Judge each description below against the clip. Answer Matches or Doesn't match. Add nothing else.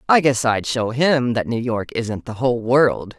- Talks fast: Matches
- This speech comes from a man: Doesn't match